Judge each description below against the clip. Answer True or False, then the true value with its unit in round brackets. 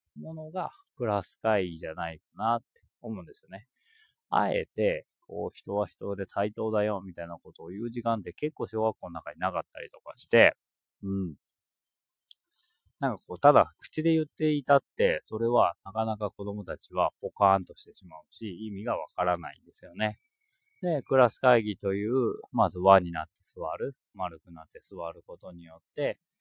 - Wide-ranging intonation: True (7.2 semitones)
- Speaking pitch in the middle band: False (105 Hz)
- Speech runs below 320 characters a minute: False (345 characters per minute)